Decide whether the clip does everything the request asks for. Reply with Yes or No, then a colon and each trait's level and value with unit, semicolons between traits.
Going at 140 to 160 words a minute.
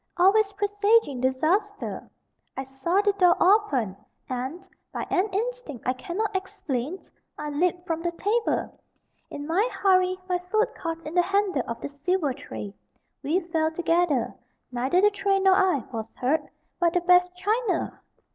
Yes: average, 155 wpm